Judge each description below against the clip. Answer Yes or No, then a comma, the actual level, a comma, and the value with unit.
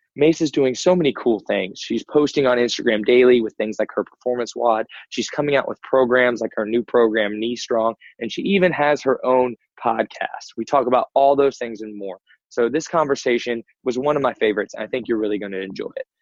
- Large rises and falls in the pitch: No, average, 3.8 semitones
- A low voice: Yes, low, 125 Hz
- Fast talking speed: Yes, fast, 225 wpm